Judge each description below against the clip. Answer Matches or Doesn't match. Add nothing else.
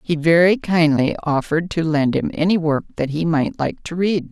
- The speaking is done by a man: Doesn't match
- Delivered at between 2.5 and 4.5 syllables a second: Doesn't match